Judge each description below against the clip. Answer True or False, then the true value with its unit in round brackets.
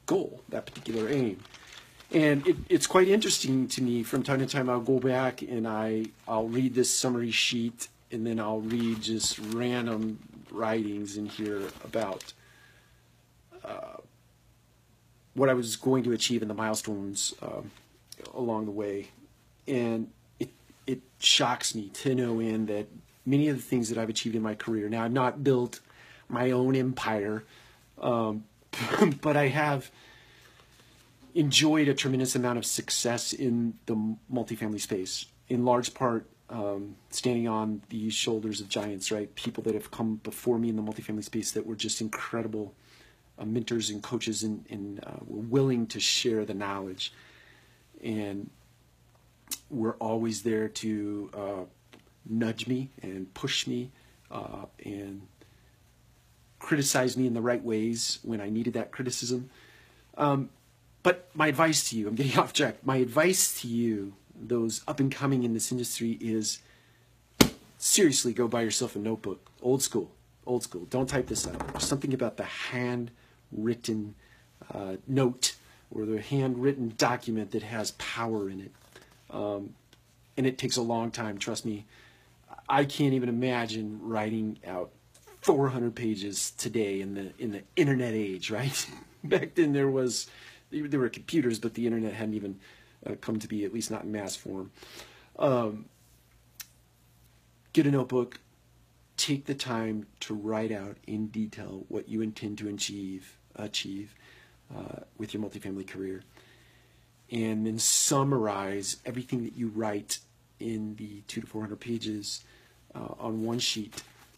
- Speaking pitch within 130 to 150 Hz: False (115 Hz)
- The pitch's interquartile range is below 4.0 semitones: True (2.7 semitones)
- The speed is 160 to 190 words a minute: False (150 wpm)